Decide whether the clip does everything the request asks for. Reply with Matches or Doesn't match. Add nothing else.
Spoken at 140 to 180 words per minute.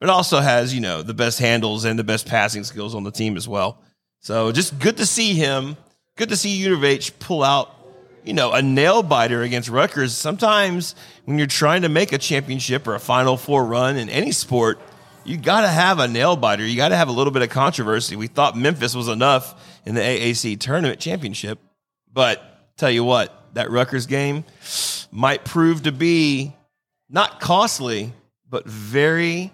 Doesn't match